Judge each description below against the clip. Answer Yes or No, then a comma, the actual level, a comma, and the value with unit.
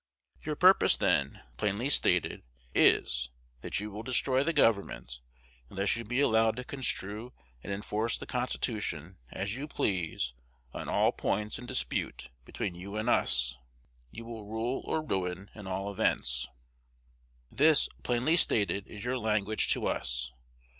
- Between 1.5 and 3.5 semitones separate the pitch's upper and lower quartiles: No, average, 4.5 semitones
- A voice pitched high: No, low, 105 Hz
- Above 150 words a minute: No, average, 145 wpm